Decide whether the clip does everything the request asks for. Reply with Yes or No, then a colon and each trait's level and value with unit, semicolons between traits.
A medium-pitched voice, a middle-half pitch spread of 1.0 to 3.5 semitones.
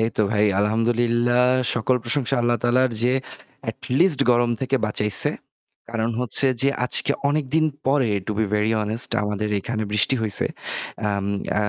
No: low, 120 Hz; average, 2.9 semitones